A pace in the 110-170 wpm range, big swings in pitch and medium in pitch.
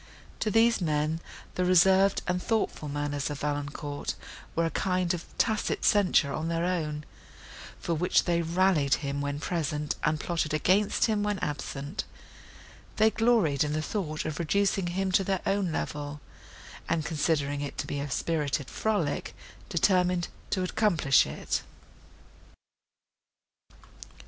No: average, 140 wpm; average, 4.3 semitones; medium, 165 Hz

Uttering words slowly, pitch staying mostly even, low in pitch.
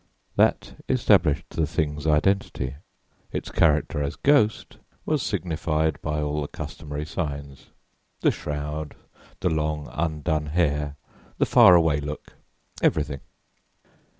Yes: slow, 115 wpm; narrow, 2.1 semitones; very low, 75 Hz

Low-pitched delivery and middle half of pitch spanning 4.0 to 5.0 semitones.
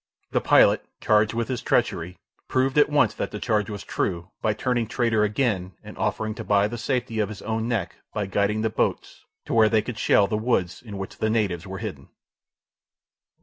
No: low, 110 Hz; narrow, 2.4 semitones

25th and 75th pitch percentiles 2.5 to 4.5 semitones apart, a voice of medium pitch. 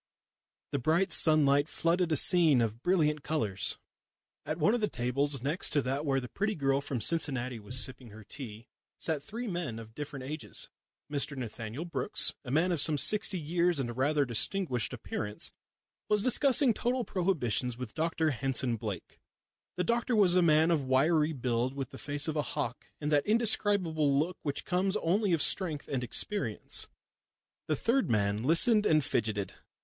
No: wide, 5.5 semitones; medium, 150 Hz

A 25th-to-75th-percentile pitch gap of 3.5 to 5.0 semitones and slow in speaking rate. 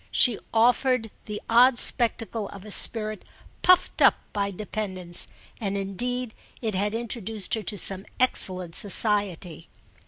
No: average, 2.9 semitones; slow, 130 wpm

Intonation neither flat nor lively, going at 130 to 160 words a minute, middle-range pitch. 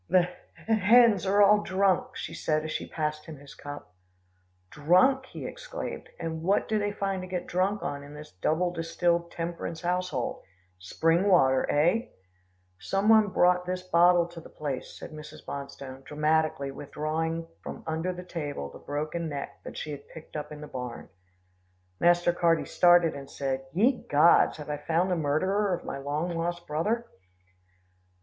No: average, 3.5 semitones; average, 170 wpm; medium, 165 Hz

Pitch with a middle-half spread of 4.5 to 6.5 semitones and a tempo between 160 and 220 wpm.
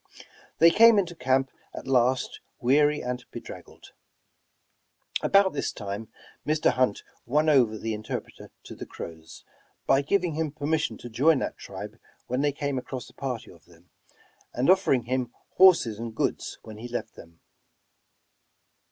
No: average, 5.0 semitones; average, 150 wpm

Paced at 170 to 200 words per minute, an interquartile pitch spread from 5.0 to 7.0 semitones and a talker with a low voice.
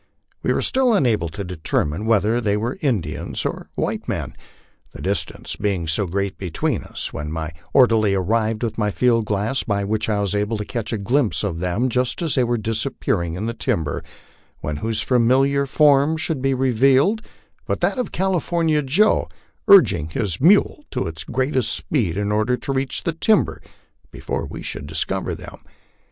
Yes: average, 175 wpm; average, 5.3 semitones; low, 115 Hz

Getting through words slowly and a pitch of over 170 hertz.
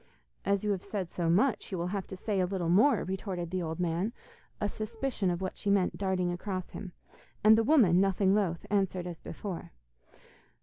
No: average, 200 wpm; high, 190 Hz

